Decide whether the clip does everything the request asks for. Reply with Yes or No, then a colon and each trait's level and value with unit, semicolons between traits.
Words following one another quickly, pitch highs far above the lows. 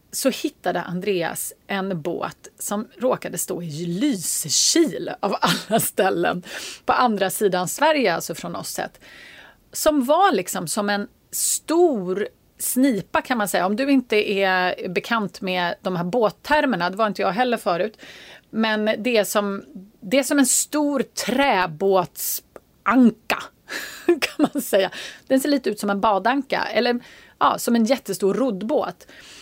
No: average, 145 wpm; wide, 5.8 semitones